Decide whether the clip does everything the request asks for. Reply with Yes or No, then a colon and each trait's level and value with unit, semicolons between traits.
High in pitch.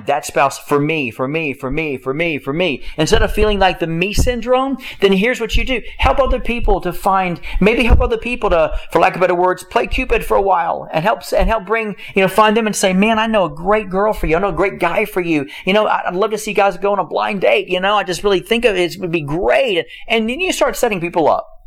Yes: high, 200 Hz